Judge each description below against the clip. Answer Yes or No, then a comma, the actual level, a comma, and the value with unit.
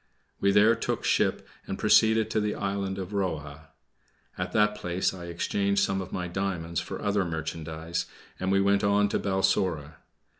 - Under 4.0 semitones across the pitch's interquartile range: Yes, average, 2.8 semitones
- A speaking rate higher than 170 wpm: No, average, 165 wpm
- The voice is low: Yes, very low, 95 Hz